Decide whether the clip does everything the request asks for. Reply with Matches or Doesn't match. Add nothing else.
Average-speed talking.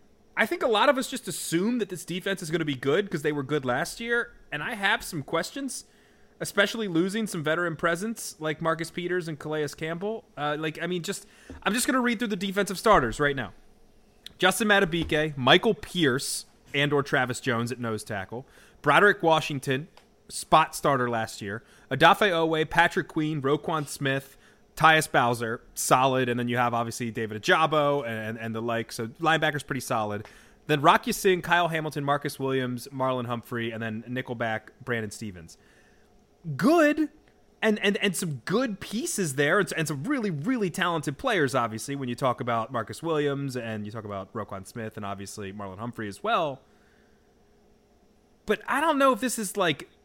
Matches